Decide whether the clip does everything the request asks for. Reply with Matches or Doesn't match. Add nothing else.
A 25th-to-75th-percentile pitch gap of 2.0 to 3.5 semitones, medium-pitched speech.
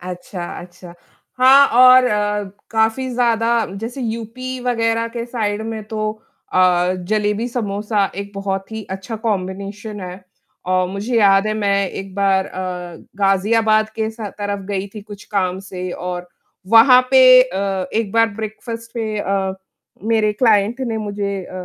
Doesn't match